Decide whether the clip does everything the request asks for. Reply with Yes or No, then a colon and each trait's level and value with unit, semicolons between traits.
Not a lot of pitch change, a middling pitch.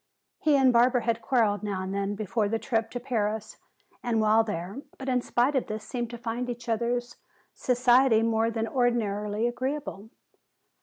No: narrow, 2.3 semitones; high, 230 Hz